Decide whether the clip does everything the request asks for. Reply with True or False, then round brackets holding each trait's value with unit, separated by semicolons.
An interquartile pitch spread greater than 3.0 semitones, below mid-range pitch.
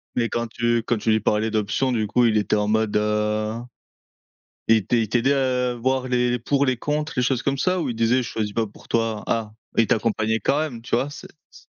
False (2.7 semitones; 115 Hz)